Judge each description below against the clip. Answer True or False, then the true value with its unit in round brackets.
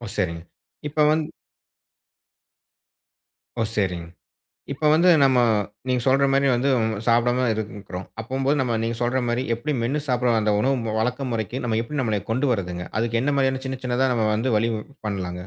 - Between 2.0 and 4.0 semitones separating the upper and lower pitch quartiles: True (3.3 semitones)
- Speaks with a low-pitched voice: True (120 Hz)